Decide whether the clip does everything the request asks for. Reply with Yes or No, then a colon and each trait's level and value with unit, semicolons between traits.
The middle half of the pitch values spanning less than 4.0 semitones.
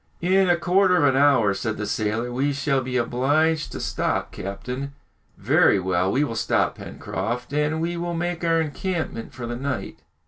No: wide, 5.4 semitones